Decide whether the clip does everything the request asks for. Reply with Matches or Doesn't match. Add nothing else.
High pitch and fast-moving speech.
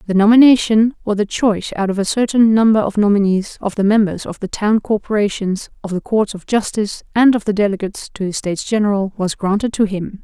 Matches